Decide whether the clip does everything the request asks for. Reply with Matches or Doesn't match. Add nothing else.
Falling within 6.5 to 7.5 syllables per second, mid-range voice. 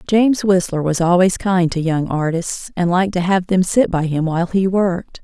Doesn't match